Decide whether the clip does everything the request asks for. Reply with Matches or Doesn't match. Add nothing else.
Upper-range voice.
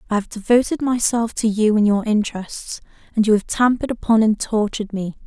Matches